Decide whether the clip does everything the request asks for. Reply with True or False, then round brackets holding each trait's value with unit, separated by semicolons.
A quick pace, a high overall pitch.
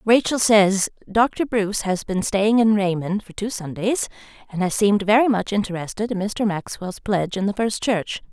False (190 wpm; 205 Hz)